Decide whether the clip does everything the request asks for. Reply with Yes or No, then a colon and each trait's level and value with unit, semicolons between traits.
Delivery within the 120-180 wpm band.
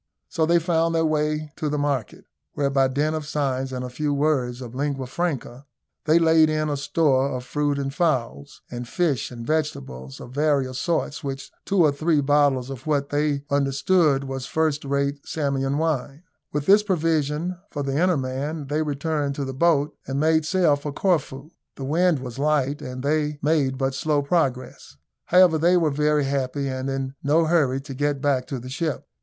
No: average, 190 wpm